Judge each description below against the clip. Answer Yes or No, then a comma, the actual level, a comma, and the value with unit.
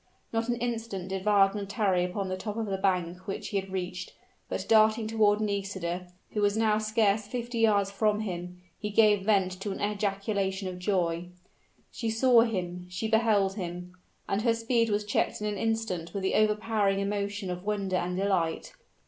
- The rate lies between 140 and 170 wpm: No, average, 180 wpm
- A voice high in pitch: Yes, high, 200 Hz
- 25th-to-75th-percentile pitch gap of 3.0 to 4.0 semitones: No, narrow, 2.5 semitones